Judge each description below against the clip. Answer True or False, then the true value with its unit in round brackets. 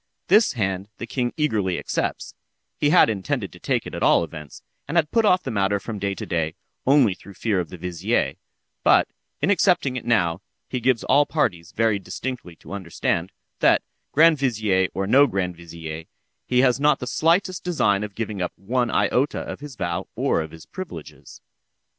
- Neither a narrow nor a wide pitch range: False (7.1 semitones)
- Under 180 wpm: False (185 wpm)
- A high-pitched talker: False (110 Hz)